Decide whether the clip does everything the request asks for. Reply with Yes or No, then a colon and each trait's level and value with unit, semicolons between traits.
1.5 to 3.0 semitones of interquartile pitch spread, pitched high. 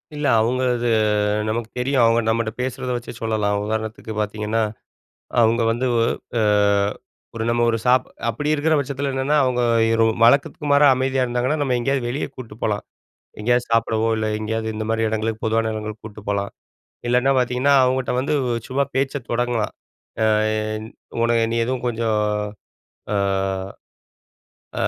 No: average, 2.7 semitones; low, 120 Hz